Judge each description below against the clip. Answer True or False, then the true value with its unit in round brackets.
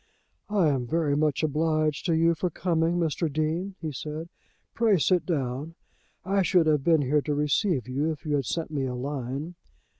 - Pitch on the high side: False (155 Hz)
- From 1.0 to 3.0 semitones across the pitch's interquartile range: True (2.7 semitones)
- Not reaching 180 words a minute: False (185 wpm)